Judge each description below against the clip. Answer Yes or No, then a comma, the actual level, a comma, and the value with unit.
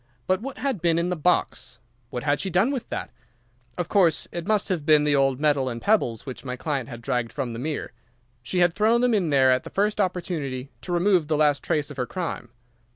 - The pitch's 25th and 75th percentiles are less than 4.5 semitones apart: No, wide, 5.5 semitones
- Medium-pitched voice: Yes, medium, 155 Hz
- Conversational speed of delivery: No, fast, 230 wpm